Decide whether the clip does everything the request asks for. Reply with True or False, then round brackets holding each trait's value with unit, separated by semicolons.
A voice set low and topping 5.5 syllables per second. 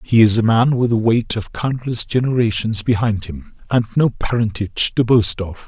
False (115 Hz; 4.9 syllables/s)